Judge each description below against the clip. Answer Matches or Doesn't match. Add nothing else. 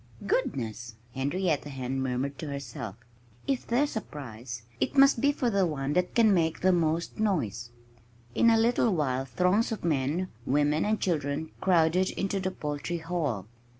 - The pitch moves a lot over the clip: Matches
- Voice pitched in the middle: Matches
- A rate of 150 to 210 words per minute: Matches